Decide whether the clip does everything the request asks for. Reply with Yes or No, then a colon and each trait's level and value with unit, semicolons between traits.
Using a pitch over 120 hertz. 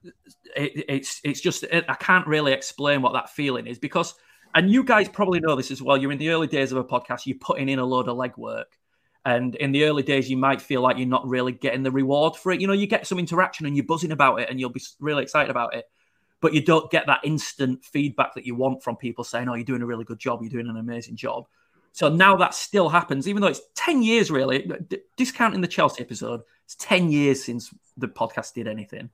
Yes: medium, 140 Hz